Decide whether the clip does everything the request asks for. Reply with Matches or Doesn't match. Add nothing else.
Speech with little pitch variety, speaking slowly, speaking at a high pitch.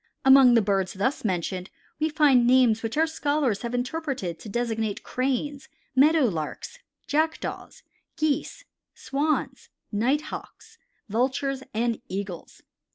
Doesn't match